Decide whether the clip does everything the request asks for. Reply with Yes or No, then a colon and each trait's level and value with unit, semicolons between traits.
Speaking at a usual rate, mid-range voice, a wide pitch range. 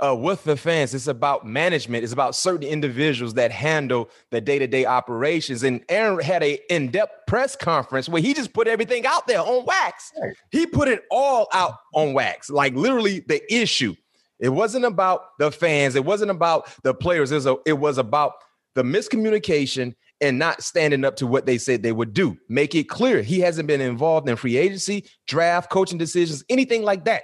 Yes: average, 195 wpm; medium, 155 Hz; wide, 6.7 semitones